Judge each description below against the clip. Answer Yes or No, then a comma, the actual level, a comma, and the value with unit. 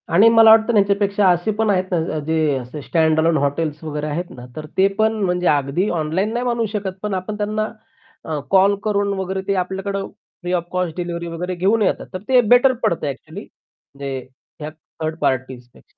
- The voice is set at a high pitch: No, medium, 180 Hz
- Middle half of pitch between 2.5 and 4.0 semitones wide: No, average, 4.4 semitones